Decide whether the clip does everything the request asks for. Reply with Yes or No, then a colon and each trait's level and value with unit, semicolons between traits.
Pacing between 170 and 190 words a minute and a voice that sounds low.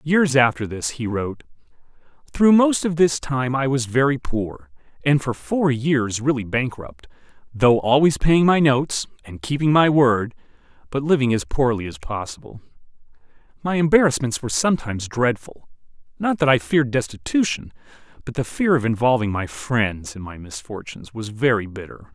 No: average, 155 wpm; low, 125 Hz